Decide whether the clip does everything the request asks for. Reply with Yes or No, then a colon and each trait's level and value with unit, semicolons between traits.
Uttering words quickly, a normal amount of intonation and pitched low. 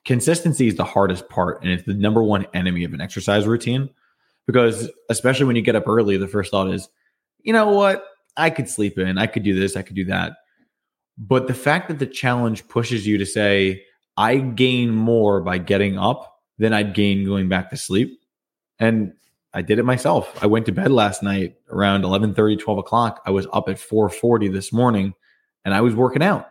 Yes: fast, 210 wpm; average, 3.9 semitones; low, 110 Hz